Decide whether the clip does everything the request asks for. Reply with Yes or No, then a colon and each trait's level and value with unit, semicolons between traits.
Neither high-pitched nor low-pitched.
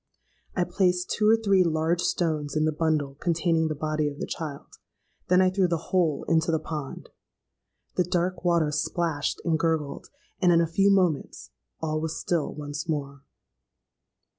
Yes: medium, 165 Hz